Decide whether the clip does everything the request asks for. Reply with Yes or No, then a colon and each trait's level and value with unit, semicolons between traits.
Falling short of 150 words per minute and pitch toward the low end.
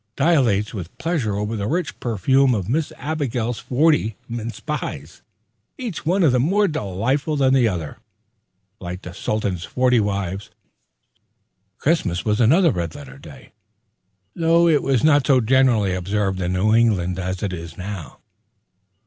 Yes: average, 140 wpm; low, 110 Hz